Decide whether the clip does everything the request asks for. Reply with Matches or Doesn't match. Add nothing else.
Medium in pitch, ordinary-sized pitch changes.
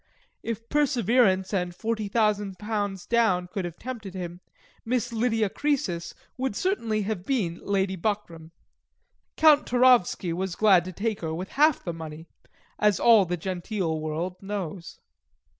Doesn't match